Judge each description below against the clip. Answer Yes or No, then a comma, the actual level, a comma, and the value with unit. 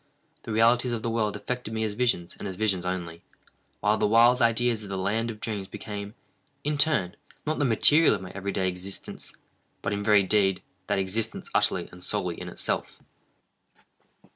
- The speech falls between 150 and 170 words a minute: No, average, 185 wpm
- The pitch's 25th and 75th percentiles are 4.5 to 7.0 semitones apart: No, average, 3.3 semitones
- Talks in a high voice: No, low, 105 Hz